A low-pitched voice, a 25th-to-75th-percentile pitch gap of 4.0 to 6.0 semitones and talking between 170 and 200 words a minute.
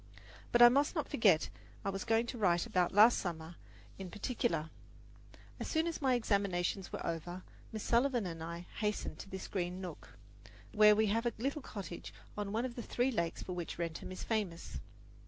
No: high, 200 Hz; average, 5.2 semitones; average, 195 wpm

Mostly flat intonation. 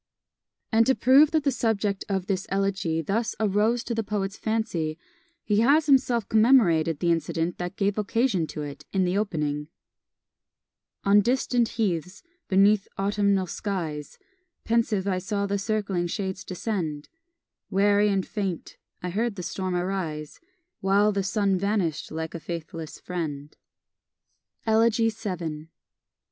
No: average, 3.9 semitones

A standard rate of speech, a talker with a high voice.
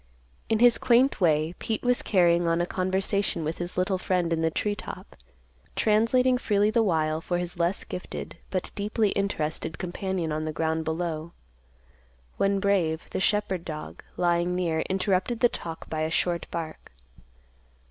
No: average, 160 wpm; medium, 180 Hz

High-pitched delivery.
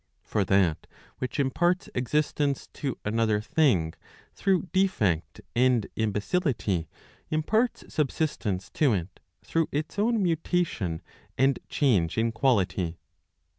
No: low, 130 Hz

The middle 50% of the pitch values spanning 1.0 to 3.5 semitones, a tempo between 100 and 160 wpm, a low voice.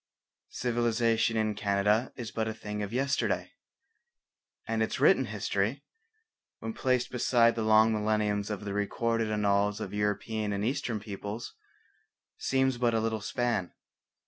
Yes: narrow, 2.4 semitones; average, 140 wpm; low, 110 Hz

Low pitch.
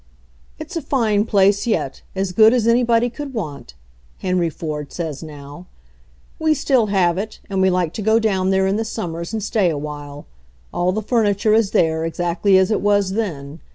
No: high, 190 Hz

